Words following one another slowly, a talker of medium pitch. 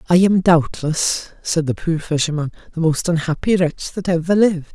No: average, 175 wpm; medium, 165 Hz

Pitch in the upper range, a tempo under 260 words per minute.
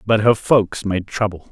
No: low, 100 Hz; average, 200 wpm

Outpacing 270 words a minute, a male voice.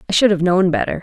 No: fast, 295 wpm; female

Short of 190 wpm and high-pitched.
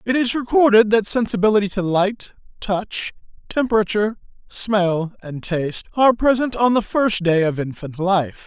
Yes: average, 150 wpm; high, 205 Hz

